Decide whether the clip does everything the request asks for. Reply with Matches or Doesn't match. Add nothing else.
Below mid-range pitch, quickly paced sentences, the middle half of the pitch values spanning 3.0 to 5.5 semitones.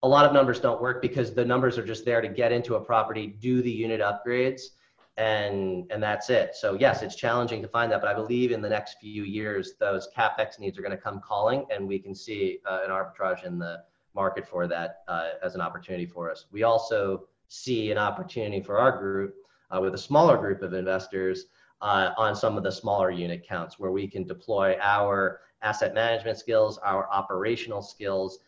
Matches